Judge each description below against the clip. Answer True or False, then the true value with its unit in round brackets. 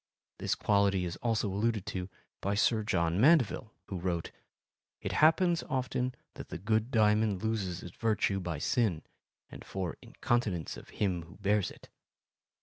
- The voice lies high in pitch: False (105 Hz)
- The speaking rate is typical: True (150 wpm)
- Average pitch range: True (3.7 semitones)